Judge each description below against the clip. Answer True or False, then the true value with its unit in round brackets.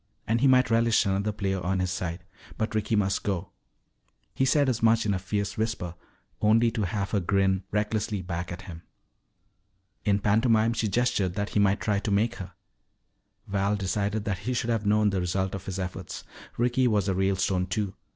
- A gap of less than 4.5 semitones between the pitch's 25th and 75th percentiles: True (2.5 semitones)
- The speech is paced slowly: False (190 wpm)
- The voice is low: True (100 Hz)